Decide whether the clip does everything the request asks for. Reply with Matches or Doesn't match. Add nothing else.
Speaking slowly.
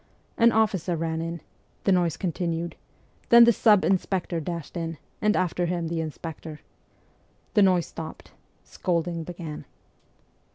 Matches